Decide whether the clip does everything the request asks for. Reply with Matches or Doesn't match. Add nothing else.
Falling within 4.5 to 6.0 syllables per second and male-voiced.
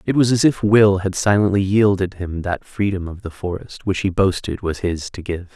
Matches